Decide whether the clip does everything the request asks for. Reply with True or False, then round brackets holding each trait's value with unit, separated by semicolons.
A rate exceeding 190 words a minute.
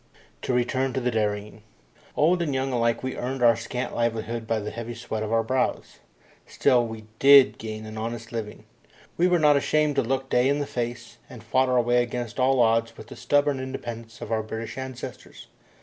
True (200 wpm)